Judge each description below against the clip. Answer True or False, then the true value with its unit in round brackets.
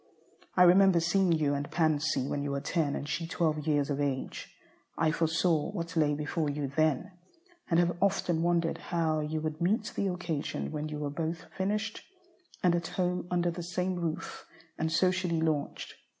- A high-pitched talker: False (165 Hz)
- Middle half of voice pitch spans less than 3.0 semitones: True (2.6 semitones)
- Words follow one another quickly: False (180 wpm)